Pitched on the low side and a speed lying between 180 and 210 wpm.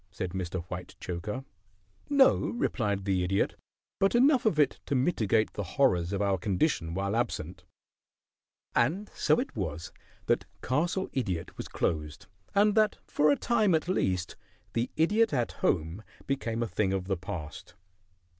No: low, 110 Hz; average, 150 wpm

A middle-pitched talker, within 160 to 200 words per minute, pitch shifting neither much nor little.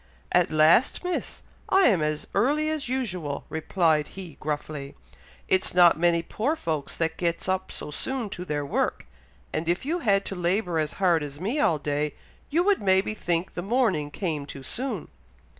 No: medium, 175 Hz; average, 175 wpm; wide, 5.9 semitones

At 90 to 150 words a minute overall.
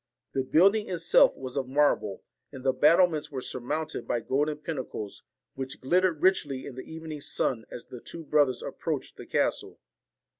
No: average, 175 wpm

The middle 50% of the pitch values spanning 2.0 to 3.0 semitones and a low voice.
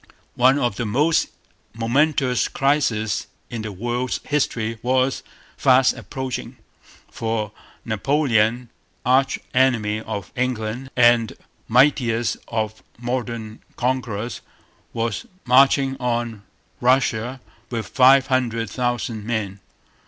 Yes: average, 2.7 semitones; low, 120 Hz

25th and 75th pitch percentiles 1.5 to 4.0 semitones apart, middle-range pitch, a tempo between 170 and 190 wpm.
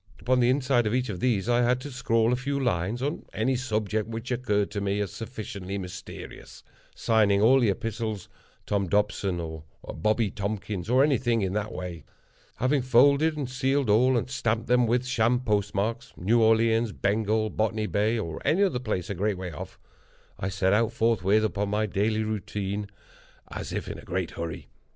No: average, 3.4 semitones; low, 110 Hz; average, 180 wpm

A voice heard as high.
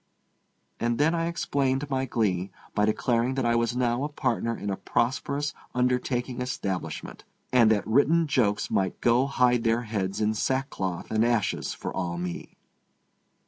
No: low, 120 Hz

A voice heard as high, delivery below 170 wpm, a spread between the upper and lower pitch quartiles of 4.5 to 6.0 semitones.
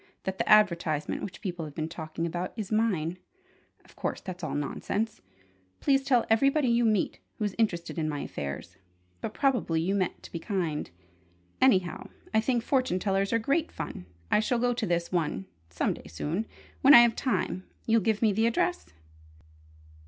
No: high, 195 Hz; average, 175 wpm; wide, 5.4 semitones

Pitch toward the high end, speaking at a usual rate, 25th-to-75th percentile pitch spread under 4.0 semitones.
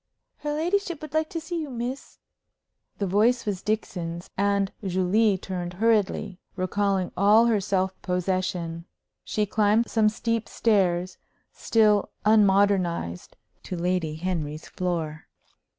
No: high, 200 Hz; slow, 120 wpm; average, 3.5 semitones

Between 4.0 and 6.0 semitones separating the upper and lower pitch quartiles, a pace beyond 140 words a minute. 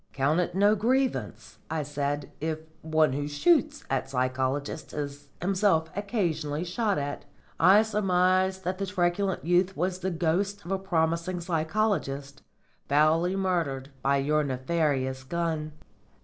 No: average, 4.7 semitones; slow, 135 wpm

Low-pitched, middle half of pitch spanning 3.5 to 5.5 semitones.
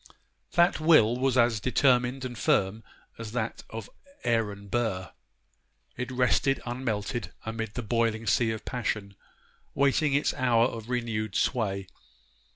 No: low, 115 Hz; narrow, 2.6 semitones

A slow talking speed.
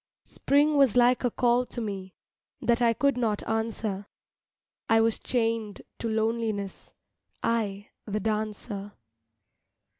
Yes: slow, 120 wpm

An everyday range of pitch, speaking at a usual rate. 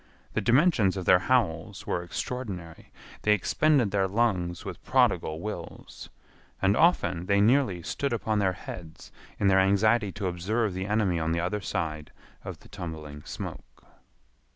Yes: average, 3.9 semitones; average, 155 wpm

